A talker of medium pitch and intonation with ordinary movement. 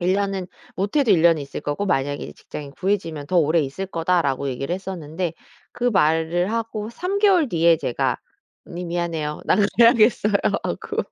Yes: medium, 175 Hz; average, 4.5 semitones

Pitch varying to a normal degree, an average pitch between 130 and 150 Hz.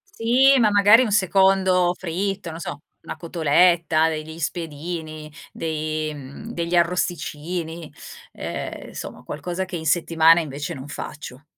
No: average, 3.0 semitones; medium, 165 Hz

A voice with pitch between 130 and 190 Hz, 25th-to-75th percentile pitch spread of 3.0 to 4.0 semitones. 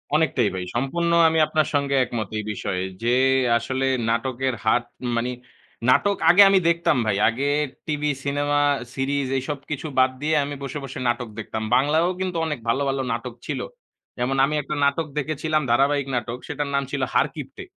Yes: medium, 140 Hz; average, 3.5 semitones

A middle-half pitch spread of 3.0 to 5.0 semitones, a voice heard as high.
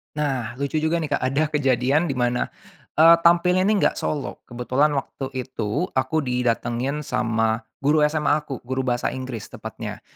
No: average, 3.5 semitones; low, 135 Hz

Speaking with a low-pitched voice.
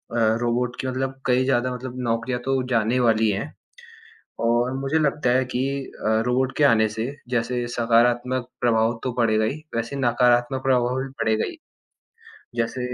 Yes: low, 125 Hz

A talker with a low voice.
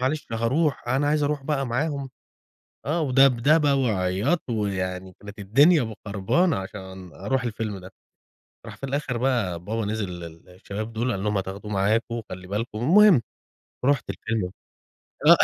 Yes: low, 115 Hz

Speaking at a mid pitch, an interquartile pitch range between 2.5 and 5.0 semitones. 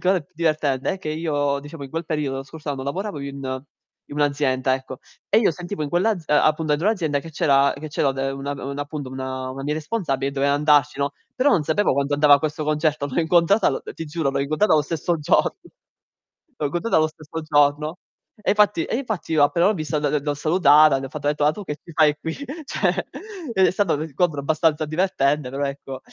Yes: medium, 150 Hz; average, 2.8 semitones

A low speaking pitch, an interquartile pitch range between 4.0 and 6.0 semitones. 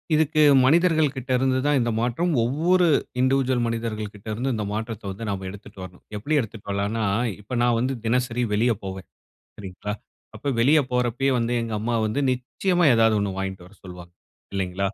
Yes: low, 115 Hz; average, 4.5 semitones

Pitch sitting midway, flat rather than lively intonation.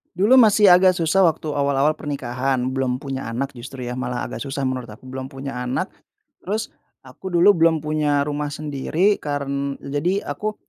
No: medium, 145 Hz; average, 4.1 semitones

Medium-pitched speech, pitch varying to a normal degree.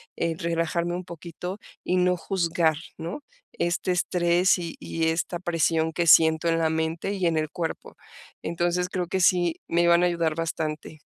No: medium, 170 Hz; narrow, 1.5 semitones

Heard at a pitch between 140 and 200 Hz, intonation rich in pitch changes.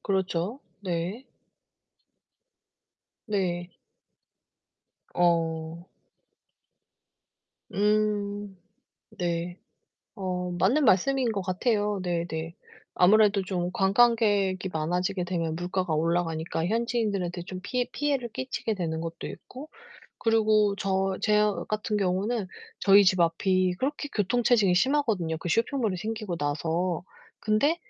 No: high, 190 Hz; average, 3.6 semitones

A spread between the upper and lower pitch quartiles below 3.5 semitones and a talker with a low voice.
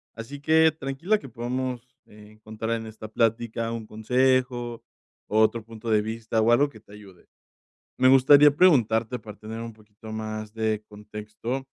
Yes: average, 2.9 semitones; low, 115 Hz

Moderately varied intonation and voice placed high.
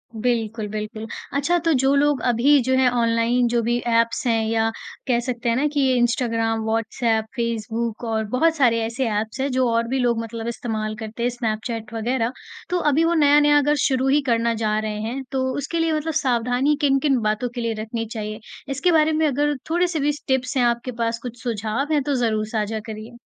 Yes: average, 3.3 semitones; high, 240 Hz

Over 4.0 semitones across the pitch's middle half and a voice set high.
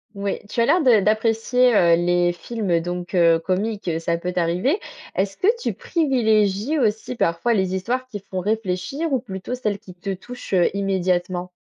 Yes: average, 4.6 semitones; high, 200 Hz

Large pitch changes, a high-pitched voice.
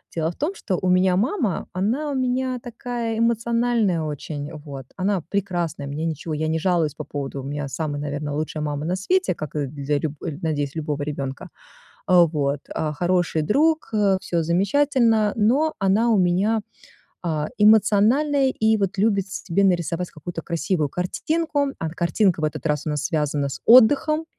No: wide, 6.7 semitones; medium, 180 Hz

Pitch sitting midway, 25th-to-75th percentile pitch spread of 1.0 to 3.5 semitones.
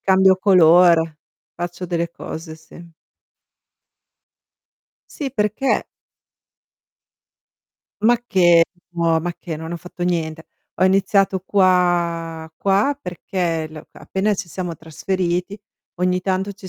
Yes: medium, 180 Hz; narrow, 2.4 semitones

